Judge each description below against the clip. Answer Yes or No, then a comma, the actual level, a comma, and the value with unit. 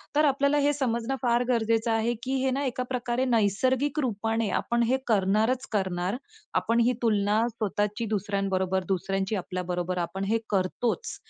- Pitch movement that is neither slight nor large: Yes, average, 4.3 semitones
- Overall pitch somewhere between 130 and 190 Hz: No, high, 225 Hz